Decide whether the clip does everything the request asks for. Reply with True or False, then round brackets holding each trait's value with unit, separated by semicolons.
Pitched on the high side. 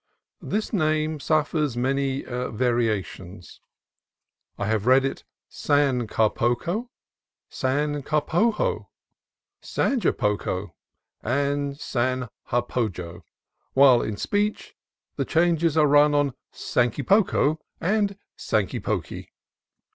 False (140 Hz)